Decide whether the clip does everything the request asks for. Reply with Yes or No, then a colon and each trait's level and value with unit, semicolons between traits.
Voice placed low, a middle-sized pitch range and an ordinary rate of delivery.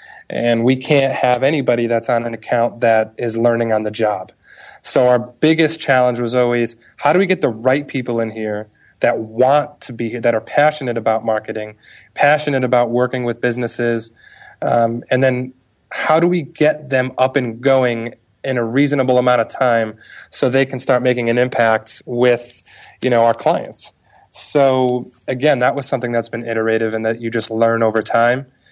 No: low, 120 Hz; narrow, 2.3 semitones; average, 185 wpm